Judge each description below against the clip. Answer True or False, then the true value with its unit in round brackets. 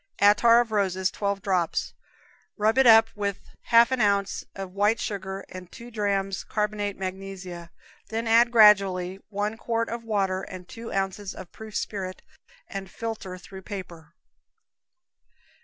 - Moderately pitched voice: False (200 Hz)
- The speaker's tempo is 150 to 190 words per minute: False (140 wpm)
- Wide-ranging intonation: False (2.7 semitones)